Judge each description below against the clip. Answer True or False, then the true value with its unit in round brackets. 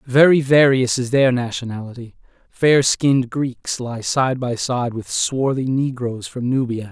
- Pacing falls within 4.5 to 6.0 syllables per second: False (4.2 syllables/s)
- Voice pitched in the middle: False (125 Hz)